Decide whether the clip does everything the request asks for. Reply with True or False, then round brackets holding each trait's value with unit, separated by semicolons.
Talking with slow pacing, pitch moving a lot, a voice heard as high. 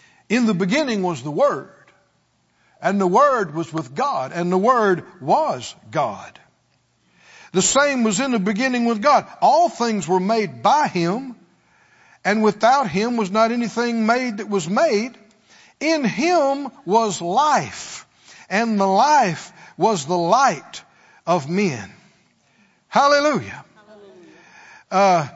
False (130 wpm; 4.6 semitones; 220 Hz)